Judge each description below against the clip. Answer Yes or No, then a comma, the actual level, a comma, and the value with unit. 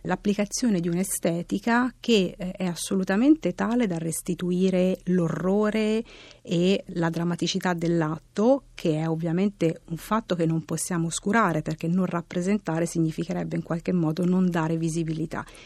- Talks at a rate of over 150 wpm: No, average, 125 wpm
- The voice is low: No, medium, 180 Hz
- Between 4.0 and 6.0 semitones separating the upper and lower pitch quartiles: No, average, 3.0 semitones